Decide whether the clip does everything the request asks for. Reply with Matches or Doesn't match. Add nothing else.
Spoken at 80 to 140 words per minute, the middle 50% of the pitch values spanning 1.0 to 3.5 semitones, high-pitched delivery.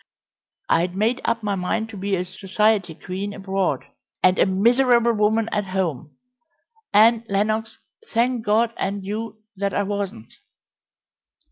Matches